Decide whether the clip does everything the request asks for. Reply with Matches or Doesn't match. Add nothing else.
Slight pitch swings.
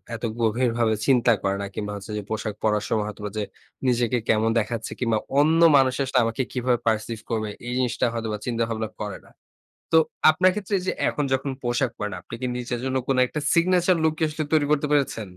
Doesn't match